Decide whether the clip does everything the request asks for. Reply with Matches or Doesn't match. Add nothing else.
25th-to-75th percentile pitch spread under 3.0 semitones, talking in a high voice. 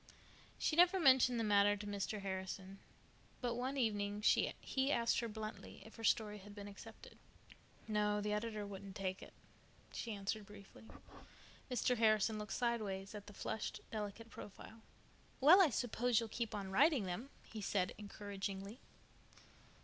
Matches